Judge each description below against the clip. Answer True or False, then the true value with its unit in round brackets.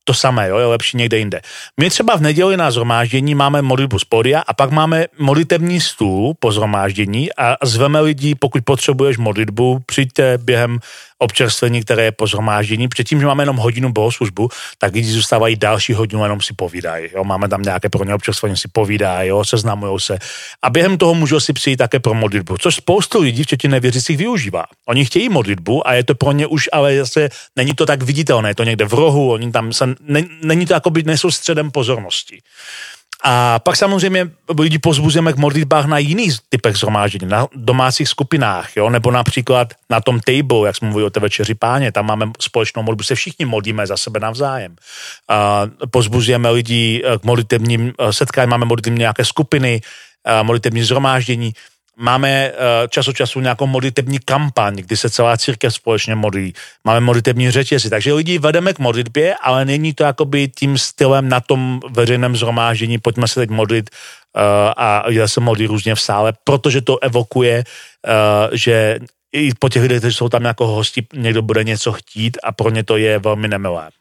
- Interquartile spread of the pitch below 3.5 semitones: False (4.0 semitones)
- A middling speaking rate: False (180 wpm)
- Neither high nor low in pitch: False (120 Hz)